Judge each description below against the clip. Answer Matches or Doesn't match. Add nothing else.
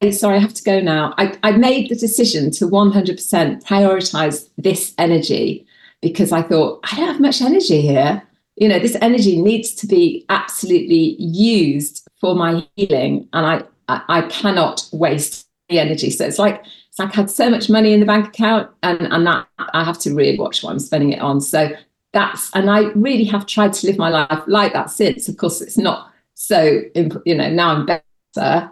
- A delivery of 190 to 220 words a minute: Matches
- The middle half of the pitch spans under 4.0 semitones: Doesn't match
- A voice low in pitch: Doesn't match